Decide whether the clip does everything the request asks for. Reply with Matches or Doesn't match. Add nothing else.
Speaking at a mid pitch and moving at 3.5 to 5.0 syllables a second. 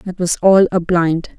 Matches